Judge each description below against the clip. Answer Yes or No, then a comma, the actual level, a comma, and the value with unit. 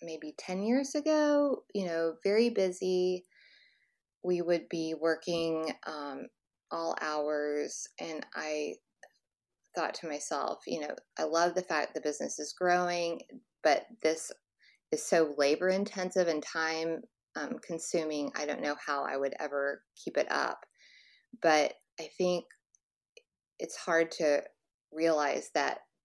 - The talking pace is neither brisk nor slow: No, slow, 130 wpm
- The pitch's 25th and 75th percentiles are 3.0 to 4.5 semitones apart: Yes, average, 3.4 semitones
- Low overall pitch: No, medium, 165 Hz